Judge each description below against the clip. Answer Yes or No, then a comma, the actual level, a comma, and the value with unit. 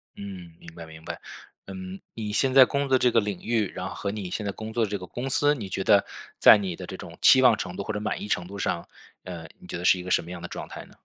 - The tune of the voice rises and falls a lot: No, average, 3.6 semitones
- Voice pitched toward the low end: Yes, low, 100 Hz